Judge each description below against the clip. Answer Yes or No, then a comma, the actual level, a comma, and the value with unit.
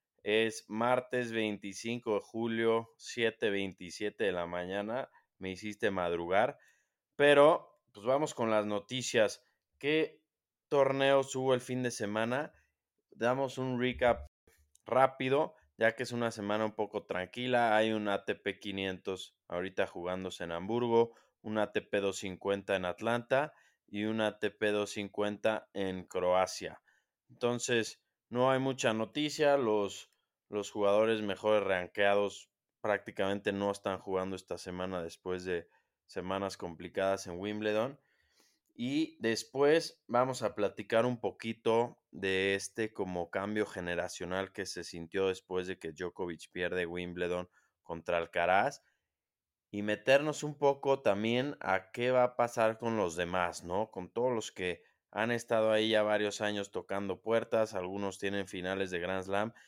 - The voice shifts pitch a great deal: No, average, 3.9 semitones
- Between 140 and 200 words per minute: No, average, 130 wpm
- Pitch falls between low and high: No, low, 105 Hz